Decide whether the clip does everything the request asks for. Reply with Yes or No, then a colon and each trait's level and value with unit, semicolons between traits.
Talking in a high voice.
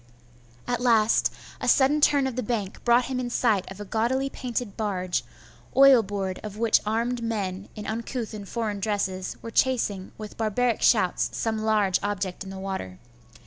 Yes: high, 220 Hz